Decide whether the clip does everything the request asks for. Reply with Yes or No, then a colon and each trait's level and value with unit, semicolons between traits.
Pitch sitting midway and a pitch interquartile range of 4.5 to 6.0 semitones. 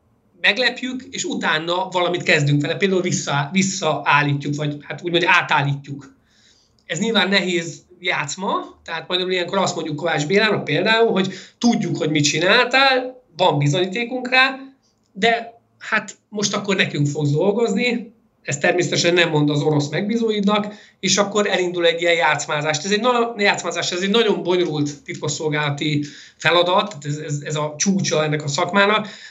Yes: medium, 175 Hz; average, 5.3 semitones